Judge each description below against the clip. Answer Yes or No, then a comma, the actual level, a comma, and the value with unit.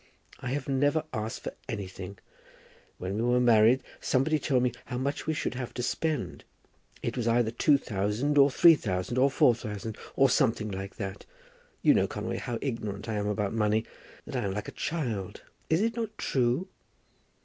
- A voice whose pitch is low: Yes, low, 120 Hz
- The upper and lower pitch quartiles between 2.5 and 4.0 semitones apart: No, average, 4.7 semitones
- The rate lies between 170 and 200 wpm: Yes, average, 185 wpm